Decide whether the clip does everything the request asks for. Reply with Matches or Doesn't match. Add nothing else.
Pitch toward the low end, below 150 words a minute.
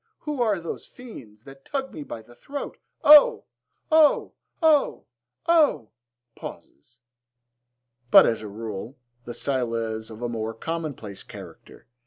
Matches